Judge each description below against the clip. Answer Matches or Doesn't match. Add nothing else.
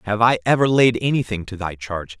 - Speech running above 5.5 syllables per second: Matches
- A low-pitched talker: Matches